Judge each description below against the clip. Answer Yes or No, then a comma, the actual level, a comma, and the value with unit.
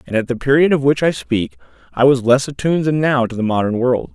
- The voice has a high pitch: No, low, 130 Hz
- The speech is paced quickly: Yes, fast, 260 wpm